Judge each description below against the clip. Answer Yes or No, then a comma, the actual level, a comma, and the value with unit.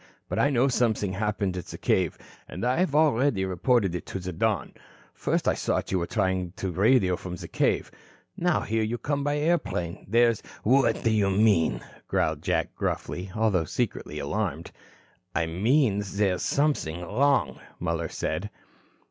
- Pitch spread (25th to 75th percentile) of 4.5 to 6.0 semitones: Yes, wide, 5.5 semitones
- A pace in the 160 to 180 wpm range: Yes, average, 165 wpm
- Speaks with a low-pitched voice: Yes, low, 105 Hz